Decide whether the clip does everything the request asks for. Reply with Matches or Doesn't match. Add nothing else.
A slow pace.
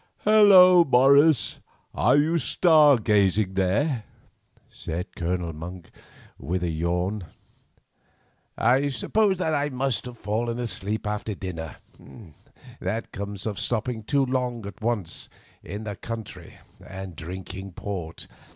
Matches